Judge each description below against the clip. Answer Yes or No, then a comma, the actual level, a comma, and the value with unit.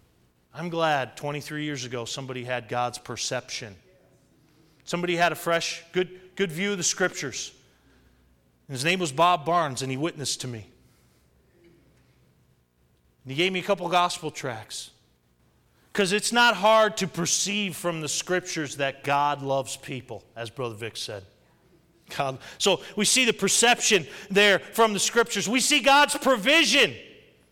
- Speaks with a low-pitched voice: No, medium, 160 Hz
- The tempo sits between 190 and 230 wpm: No, average, 150 wpm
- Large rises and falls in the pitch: Yes, wide, 7.3 semitones